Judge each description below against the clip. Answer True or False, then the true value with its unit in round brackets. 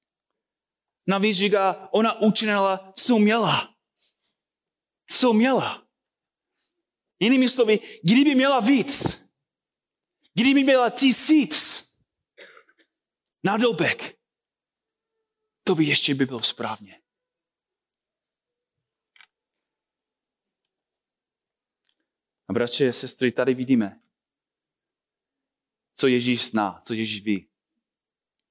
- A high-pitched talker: True (205 Hz)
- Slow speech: True (75 wpm)